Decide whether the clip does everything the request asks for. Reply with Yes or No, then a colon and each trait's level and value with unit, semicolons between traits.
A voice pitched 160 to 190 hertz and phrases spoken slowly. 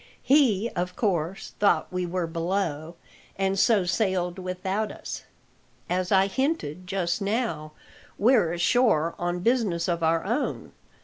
Yes: medium, 185 Hz; slow, 130 wpm